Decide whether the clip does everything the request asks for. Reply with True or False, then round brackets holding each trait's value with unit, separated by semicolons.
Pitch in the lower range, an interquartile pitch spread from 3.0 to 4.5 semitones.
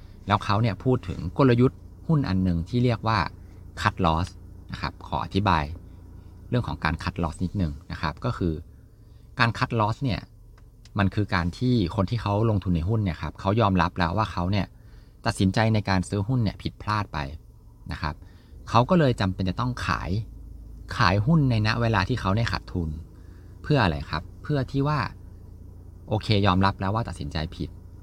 True (95 Hz; 4.0 semitones)